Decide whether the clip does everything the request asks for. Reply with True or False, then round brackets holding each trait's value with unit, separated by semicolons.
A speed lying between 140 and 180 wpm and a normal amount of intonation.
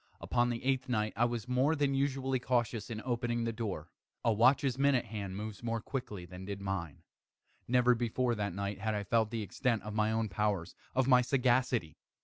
False (195 wpm; 3.3 semitones)